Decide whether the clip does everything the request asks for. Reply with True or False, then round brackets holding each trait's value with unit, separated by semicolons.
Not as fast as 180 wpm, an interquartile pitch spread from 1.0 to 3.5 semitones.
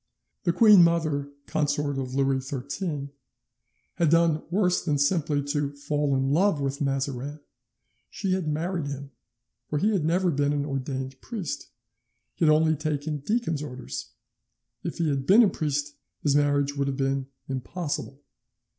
True (155 wpm; 3.1 semitones)